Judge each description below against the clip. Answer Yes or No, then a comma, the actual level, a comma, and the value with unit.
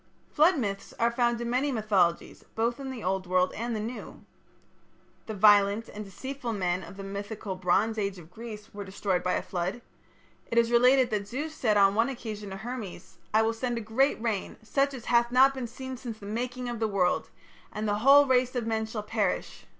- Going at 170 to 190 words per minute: No, fast, 205 wpm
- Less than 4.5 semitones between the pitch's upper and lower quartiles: Yes, average, 3.5 semitones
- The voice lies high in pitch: Yes, high, 220 Hz